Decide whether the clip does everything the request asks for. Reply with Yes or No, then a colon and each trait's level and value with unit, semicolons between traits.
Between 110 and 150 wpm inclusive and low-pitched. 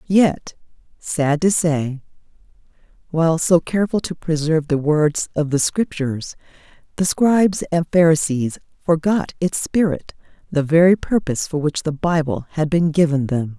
No: average, 140 wpm; medium, 160 Hz